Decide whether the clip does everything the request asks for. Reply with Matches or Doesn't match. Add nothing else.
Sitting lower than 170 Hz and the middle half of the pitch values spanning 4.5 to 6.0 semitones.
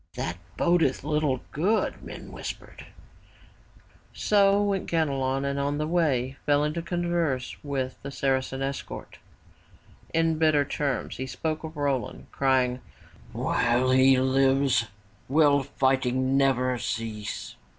Doesn't match